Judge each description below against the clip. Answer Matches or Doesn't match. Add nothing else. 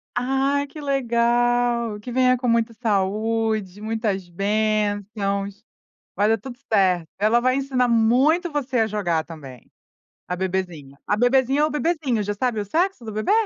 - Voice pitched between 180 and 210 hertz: Doesn't match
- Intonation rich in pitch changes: Doesn't match